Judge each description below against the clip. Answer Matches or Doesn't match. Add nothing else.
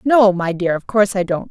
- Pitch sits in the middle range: Doesn't match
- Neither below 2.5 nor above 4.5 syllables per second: Doesn't match